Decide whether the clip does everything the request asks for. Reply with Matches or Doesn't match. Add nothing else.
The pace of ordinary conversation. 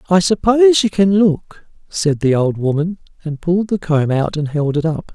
Doesn't match